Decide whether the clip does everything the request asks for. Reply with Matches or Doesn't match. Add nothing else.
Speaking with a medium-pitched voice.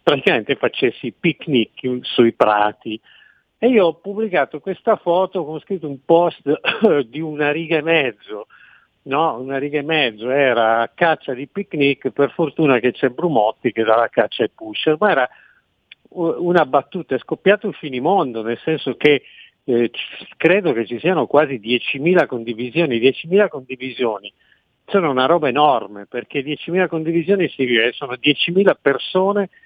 Matches